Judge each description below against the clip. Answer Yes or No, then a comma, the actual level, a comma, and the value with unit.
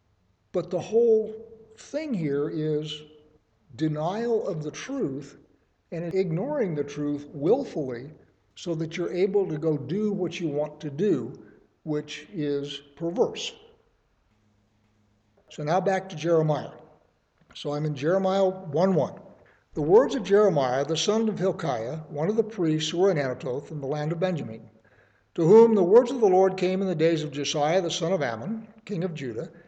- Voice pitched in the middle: Yes, medium, 165 Hz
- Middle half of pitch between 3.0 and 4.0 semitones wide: No, average, 4.9 semitones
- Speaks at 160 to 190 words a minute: Yes, average, 170 wpm